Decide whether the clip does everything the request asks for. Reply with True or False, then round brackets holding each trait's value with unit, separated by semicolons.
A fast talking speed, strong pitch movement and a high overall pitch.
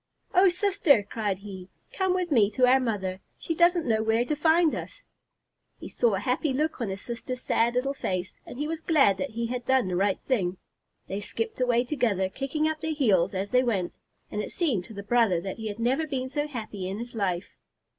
True (220 wpm; 6.6 semitones; 240 Hz)